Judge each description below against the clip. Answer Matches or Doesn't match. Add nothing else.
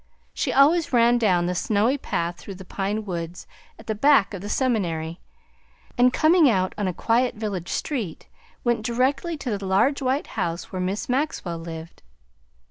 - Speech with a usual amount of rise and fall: Doesn't match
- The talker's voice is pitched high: Matches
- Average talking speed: Matches